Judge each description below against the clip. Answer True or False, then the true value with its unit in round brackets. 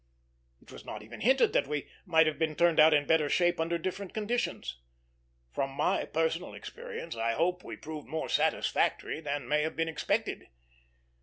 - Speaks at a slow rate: False (175 wpm)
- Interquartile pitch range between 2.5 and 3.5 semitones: True (2.9 semitones)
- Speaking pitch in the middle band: True (160 Hz)